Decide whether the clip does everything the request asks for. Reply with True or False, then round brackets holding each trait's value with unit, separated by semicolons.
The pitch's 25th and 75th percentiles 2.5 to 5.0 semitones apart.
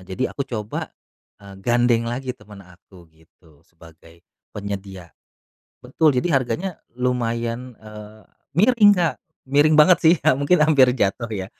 False (5.4 semitones)